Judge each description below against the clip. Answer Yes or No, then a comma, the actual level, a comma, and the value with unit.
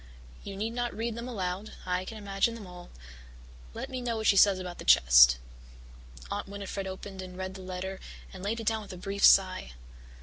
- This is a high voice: Yes, high, 195 Hz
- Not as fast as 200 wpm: No, fast, 205 wpm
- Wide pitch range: No, average, 2.9 semitones